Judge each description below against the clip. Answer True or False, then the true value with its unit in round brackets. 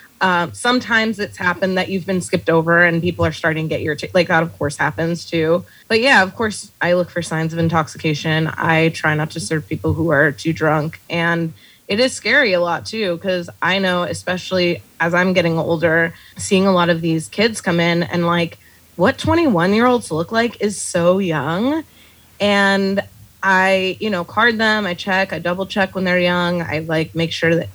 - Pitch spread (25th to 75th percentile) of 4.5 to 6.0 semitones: False (2.9 semitones)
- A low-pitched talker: False (175 Hz)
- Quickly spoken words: True (210 wpm)